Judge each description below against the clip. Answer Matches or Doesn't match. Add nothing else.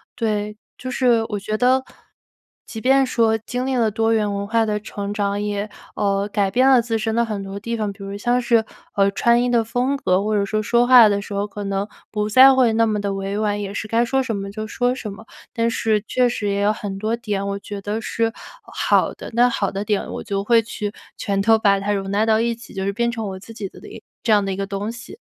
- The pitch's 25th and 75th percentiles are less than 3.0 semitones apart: Matches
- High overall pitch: Matches